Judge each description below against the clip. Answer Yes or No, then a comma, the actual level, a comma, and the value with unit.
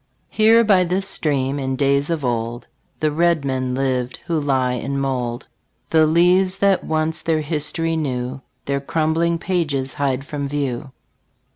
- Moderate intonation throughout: Yes, average, 3.9 semitones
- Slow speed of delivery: No, average, 150 wpm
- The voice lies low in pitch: No, medium, 145 Hz